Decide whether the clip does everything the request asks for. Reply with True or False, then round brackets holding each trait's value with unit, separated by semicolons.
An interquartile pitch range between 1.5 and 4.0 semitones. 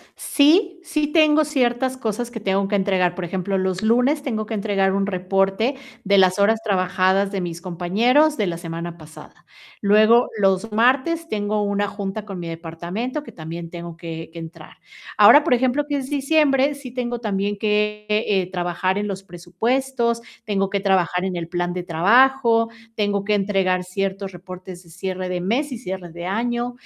False (4.8 semitones)